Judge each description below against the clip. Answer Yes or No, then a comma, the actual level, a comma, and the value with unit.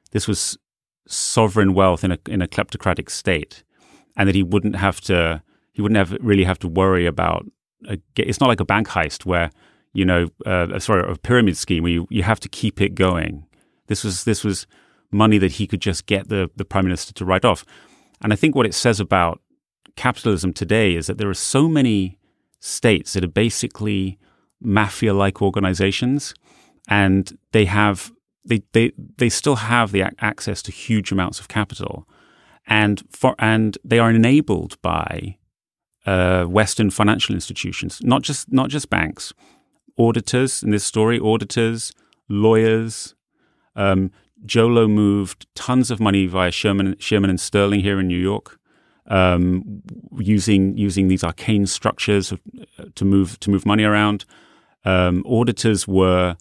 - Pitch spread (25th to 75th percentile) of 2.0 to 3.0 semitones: Yes, average, 2.7 semitones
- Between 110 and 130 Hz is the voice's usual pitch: No, low, 100 Hz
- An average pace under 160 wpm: No, average, 165 wpm